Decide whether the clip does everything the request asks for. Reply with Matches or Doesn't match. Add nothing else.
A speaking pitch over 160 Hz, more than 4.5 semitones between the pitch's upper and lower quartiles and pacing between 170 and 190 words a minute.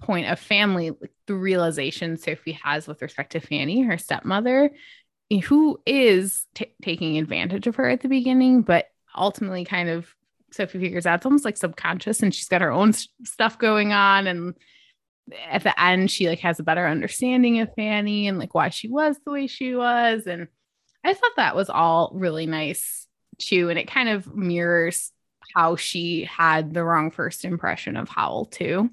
Matches